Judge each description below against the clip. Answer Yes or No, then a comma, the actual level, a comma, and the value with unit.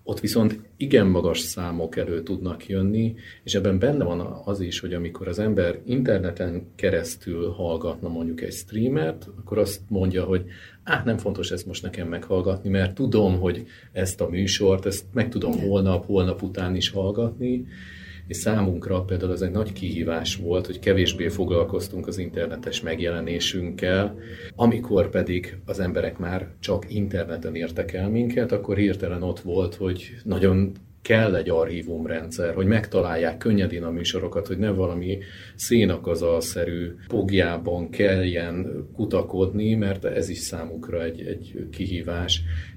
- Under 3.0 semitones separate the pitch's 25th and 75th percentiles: Yes, narrow, 2.6 semitones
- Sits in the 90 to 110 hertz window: Yes, very low, 95 Hz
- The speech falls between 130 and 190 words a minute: Yes, average, 140 wpm